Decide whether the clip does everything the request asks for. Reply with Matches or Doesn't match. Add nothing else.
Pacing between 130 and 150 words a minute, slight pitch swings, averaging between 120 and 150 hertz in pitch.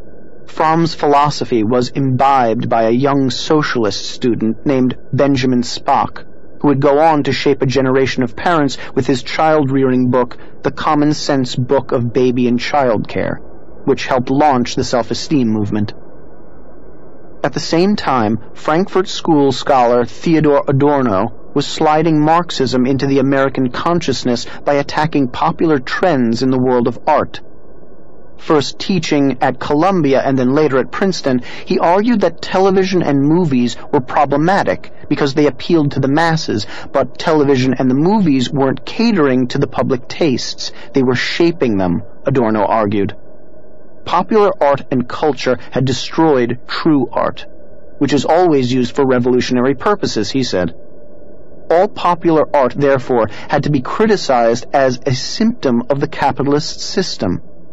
Doesn't match